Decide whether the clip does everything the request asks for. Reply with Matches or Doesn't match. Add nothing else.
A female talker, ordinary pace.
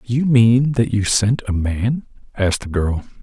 Doesn't match